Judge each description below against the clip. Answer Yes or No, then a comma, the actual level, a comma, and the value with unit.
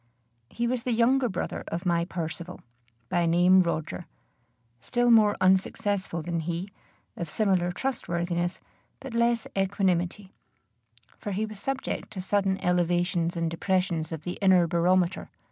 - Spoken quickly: No, slow, 135 wpm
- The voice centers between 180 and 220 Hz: Yes, medium, 185 Hz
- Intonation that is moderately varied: Yes, average, 3.0 semitones